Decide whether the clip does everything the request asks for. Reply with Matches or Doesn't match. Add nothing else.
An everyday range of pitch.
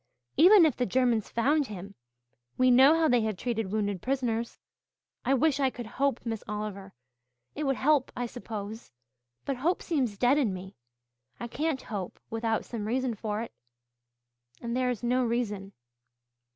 Matches